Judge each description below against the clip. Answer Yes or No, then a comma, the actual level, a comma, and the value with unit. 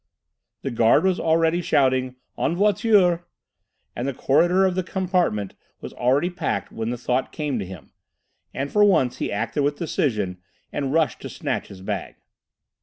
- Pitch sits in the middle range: Yes, medium, 145 Hz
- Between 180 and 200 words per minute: No, average, 165 wpm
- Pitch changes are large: Yes, wide, 6.4 semitones